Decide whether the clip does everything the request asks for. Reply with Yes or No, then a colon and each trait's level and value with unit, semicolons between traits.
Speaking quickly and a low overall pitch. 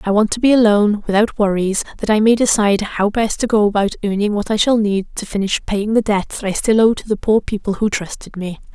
No: fast, 255 wpm; high, 210 Hz